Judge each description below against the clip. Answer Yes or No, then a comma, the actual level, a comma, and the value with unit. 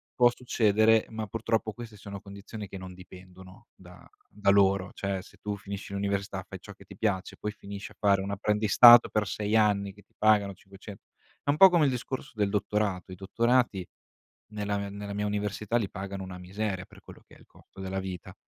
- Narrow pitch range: Yes, narrow, 1.8 semitones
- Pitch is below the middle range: Yes, low, 100 Hz